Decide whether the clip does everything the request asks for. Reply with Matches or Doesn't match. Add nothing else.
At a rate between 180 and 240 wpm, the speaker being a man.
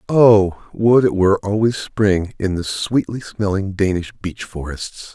Doesn't match